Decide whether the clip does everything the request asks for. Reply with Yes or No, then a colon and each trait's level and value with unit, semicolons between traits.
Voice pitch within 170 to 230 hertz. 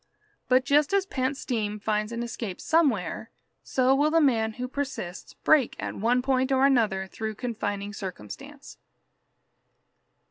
No: high, 245 Hz